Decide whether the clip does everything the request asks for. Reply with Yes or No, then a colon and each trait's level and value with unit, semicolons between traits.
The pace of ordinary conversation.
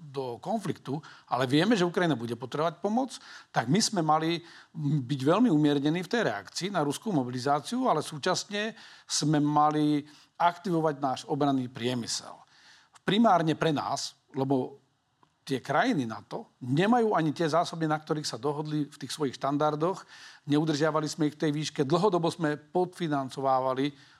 Yes: average, 145 wpm